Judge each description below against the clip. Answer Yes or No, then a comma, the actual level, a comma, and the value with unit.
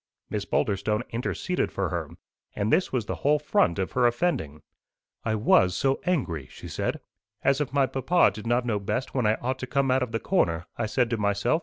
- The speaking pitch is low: Yes, low, 120 Hz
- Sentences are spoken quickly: Yes, fast, 210 wpm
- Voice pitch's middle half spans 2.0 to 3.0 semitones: No, average, 4.7 semitones